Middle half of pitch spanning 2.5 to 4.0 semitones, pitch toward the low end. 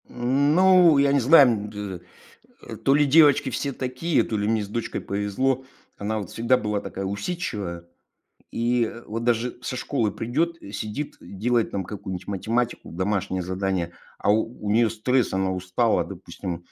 No: average, 4.8 semitones; low, 115 Hz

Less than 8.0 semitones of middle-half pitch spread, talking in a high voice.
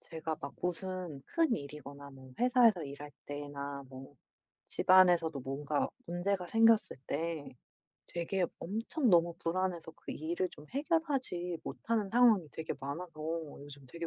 No: average, 5.2 semitones; medium, 170 Hz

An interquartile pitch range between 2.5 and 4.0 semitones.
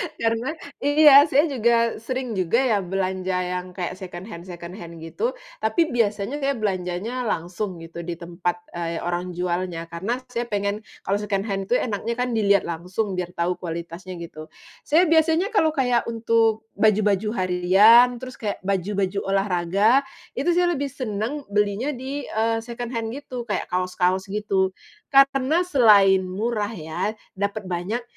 No: average, 4.9 semitones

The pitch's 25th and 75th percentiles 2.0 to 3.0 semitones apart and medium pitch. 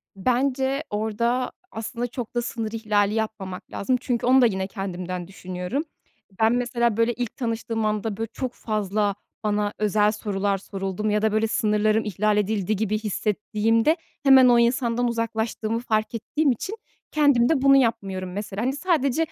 No: average, 2.7 semitones; high, 220 Hz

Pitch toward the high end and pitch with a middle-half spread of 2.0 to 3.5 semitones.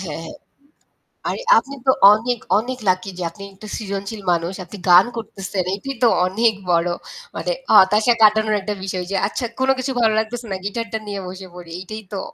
Yes: high, 205 Hz; average, 3.1 semitones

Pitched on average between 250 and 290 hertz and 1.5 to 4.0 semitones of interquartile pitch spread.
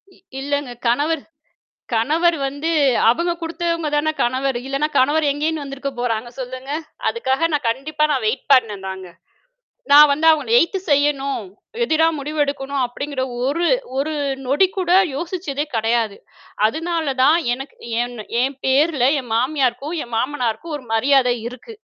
Yes: very high, 280 Hz; average, 3.7 semitones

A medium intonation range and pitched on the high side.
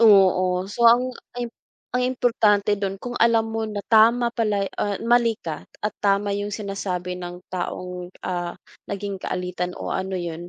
Yes: average, 3.8 semitones; high, 200 Hz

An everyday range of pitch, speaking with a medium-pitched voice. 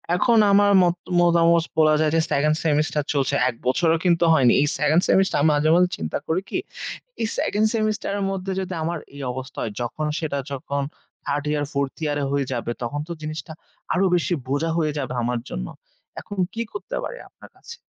Yes: average, 4.1 semitones; medium, 155 Hz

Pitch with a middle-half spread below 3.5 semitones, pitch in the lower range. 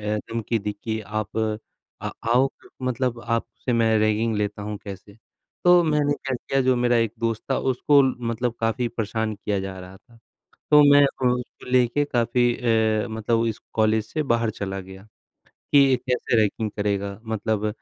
Yes: narrow, 2.6 semitones; low, 115 Hz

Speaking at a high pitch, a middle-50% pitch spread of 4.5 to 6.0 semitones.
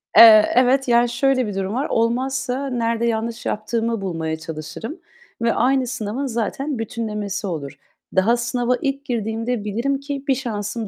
No: high, 235 Hz; average, 3.3 semitones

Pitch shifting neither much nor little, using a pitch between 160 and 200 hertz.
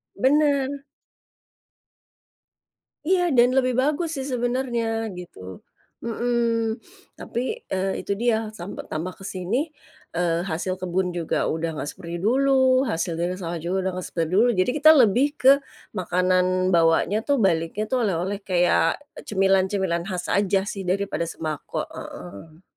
No: wide, 5.8 semitones; high, 190 Hz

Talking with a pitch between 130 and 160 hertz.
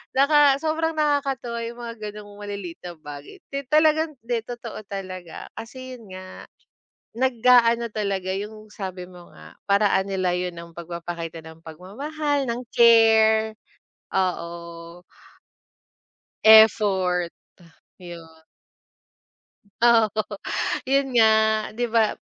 No: high, 215 Hz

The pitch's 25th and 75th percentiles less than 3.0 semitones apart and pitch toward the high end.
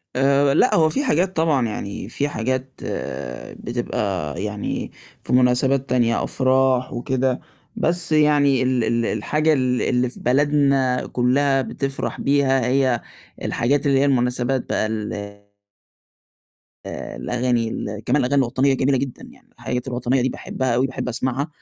No: narrow, 2.4 semitones; low, 130 Hz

